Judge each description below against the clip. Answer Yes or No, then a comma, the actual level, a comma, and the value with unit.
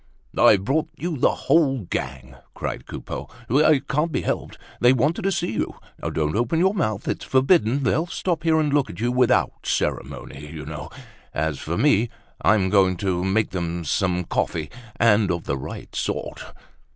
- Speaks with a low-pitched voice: Yes, low, 110 Hz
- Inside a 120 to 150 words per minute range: No, average, 175 wpm